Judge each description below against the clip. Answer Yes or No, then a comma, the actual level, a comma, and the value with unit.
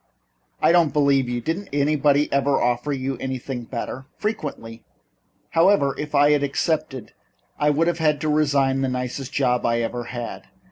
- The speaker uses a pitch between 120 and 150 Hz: Yes, medium, 140 Hz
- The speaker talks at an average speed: Yes, average, 160 wpm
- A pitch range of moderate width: Yes, average, 3.0 semitones